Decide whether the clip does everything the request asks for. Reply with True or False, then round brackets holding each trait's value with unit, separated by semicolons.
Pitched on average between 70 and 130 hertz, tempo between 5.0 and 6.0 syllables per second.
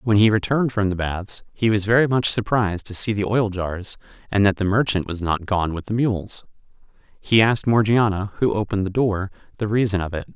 True (105 Hz; 5.6 syllables/s)